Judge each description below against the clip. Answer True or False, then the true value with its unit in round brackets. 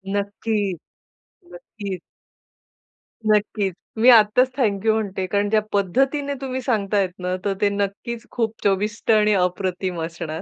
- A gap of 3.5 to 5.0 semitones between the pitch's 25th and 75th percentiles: False (2.6 semitones)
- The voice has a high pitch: True (205 Hz)